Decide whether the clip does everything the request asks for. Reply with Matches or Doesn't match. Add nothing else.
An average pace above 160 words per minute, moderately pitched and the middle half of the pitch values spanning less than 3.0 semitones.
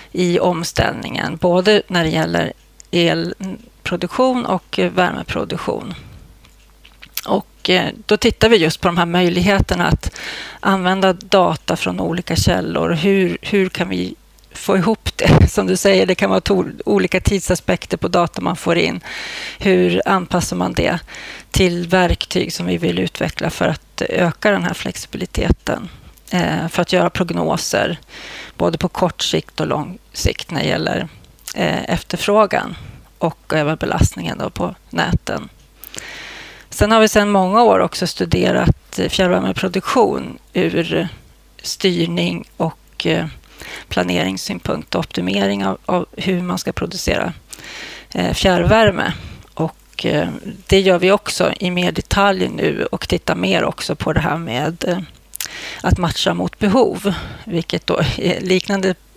Doesn't match